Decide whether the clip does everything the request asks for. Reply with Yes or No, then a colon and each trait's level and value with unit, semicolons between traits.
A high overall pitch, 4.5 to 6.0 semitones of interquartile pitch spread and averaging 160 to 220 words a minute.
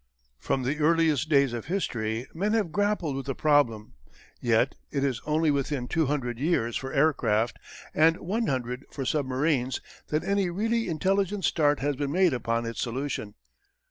No: medium, 145 Hz; average, 4.8 semitones; average, 165 wpm